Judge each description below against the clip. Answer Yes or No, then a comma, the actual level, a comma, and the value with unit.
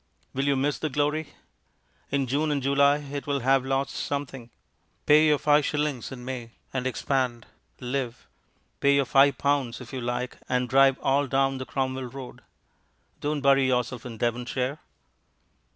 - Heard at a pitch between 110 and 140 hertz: Yes, low, 135 Hz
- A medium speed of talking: Yes, average, 160 wpm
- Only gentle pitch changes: Yes, narrow, 2.0 semitones